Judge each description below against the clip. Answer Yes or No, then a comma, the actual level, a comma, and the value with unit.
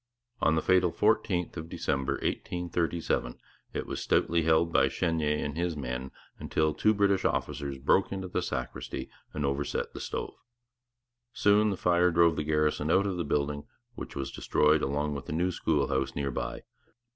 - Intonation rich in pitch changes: No, average, 3.4 semitones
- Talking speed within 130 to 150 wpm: No, average, 170 wpm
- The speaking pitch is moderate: No, very low, 80 Hz